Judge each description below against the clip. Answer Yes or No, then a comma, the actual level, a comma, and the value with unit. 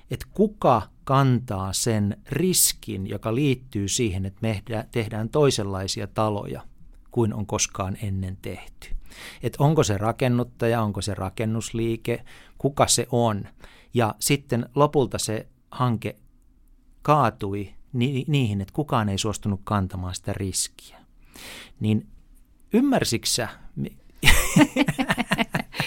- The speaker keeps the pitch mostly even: No, average, 4.3 semitones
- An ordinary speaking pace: Yes, average, 105 wpm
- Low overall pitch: Yes, low, 115 Hz